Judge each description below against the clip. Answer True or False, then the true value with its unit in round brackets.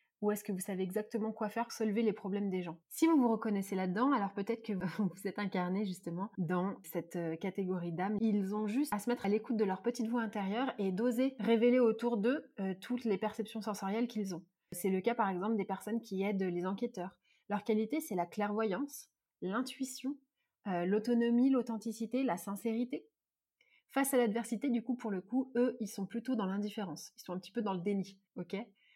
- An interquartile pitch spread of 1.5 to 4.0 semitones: True (3.4 semitones)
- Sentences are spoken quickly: False (205 wpm)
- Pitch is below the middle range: False (215 Hz)